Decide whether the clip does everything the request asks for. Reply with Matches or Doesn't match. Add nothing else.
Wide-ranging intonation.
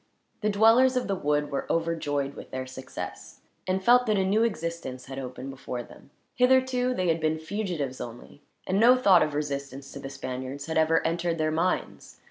Matches